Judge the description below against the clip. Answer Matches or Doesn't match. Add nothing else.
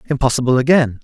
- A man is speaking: Matches